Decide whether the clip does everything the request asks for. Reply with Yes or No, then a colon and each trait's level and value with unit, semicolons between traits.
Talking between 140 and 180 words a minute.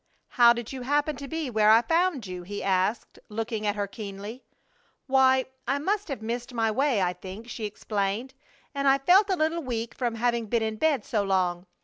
No: fast, 205 wpm